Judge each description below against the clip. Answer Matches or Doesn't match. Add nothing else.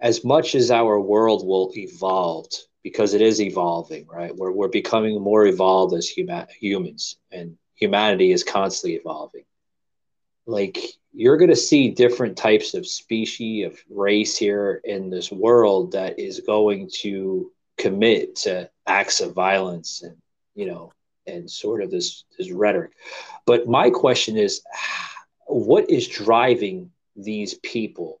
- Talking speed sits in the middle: Matches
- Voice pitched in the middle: Doesn't match